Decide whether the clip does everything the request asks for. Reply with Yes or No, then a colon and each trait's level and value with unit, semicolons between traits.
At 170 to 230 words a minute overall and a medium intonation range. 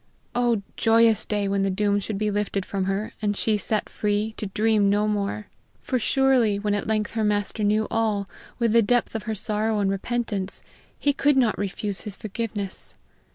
No: average, 190 wpm; narrow, 1.8 semitones